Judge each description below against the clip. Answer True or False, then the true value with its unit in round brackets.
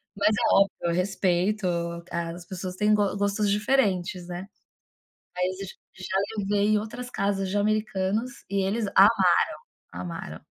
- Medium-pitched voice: False (200 Hz)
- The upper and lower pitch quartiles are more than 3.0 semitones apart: False (2.4 semitones)